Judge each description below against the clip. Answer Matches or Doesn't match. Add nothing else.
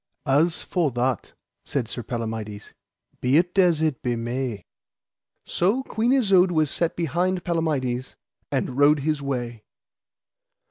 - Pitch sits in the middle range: Matches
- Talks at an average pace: Doesn't match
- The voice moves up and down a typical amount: Doesn't match